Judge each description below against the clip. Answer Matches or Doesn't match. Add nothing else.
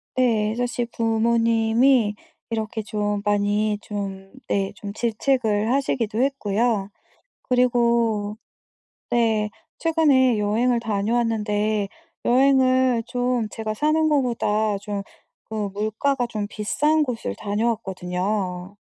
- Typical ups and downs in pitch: Matches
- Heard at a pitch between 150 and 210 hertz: Doesn't match